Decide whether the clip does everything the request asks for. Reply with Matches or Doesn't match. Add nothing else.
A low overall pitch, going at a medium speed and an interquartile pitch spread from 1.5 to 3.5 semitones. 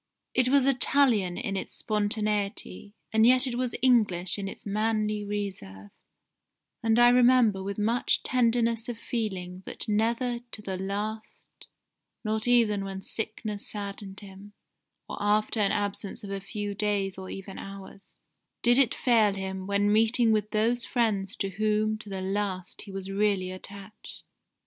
Doesn't match